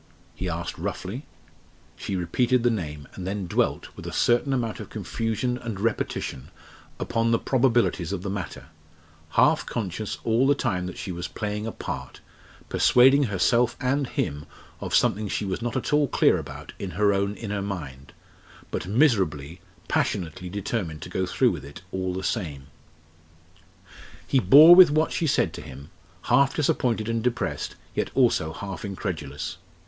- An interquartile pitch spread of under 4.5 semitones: No, average, 5.3 semitones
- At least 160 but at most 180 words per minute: Yes, average, 165 wpm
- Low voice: Yes, low, 100 Hz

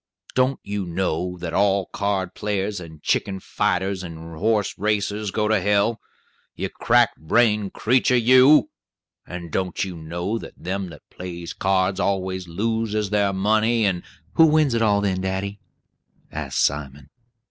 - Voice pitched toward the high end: No, low, 100 Hz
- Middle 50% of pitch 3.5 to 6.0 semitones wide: No, average, 3.0 semitones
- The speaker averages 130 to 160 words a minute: Yes, average, 150 wpm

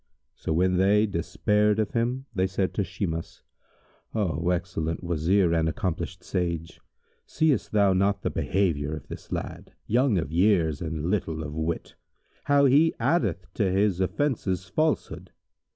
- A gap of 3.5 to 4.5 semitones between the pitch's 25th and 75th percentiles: Yes, average, 4.0 semitones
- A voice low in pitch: Yes, very low, 95 Hz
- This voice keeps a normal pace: Yes, average, 145 wpm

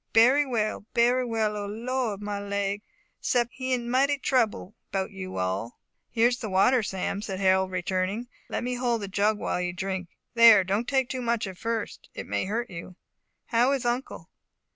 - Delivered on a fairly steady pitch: No, average, 4.1 semitones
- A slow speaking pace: No, average, 185 wpm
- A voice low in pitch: No, high, 215 Hz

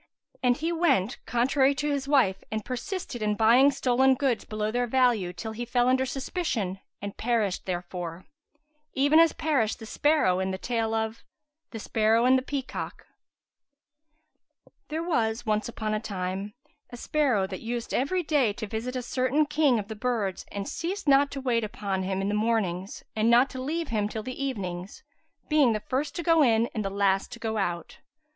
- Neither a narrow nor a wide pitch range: Yes, average, 4.4 semitones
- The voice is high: Yes, high, 235 Hz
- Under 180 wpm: No, average, 185 wpm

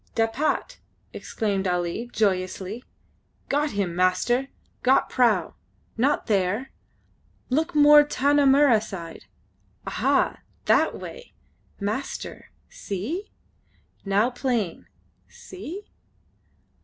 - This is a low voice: No, high, 230 Hz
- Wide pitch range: Yes, wide, 6.6 semitones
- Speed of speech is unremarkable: No, slow, 85 wpm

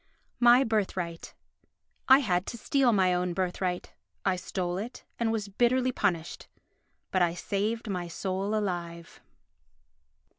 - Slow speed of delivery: Yes, slow, 125 wpm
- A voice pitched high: Yes, high, 195 Hz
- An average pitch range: Yes, average, 4.1 semitones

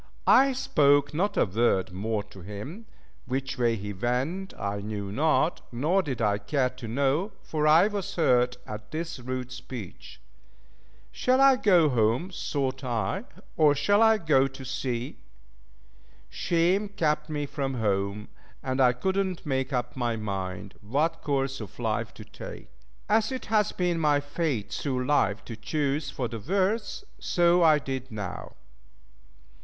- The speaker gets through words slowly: No, average, 155 wpm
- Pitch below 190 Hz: Yes, low, 135 Hz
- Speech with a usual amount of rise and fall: No, wide, 6.5 semitones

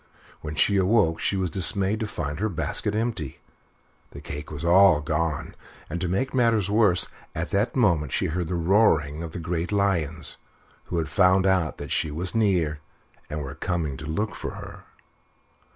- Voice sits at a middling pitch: No, very low, 85 Hz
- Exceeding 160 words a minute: Yes, average, 180 wpm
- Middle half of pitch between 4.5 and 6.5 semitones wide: No, average, 4.1 semitones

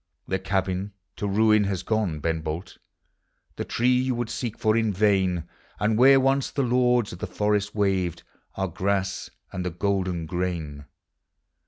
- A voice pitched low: Yes, low, 100 Hz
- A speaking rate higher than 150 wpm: Yes, average, 160 wpm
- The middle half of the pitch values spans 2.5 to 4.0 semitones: Yes, average, 3.4 semitones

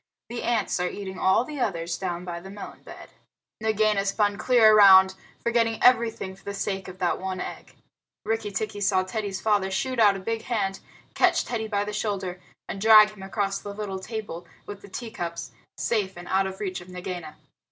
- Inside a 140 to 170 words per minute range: No, average, 195 wpm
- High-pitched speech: Yes, high, 200 Hz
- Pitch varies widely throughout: No, narrow, 2.4 semitones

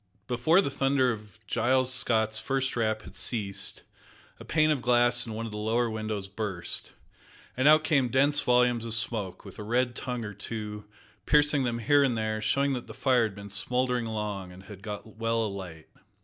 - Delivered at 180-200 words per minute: Yes, average, 190 wpm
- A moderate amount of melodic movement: Yes, average, 3.3 semitones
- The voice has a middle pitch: No, low, 115 Hz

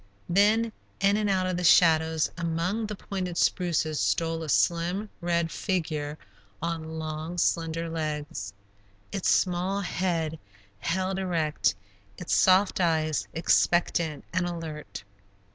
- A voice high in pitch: No, medium, 170 Hz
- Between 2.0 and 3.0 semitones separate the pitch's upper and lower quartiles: Yes, narrow, 2.5 semitones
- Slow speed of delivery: Yes, slow, 120 wpm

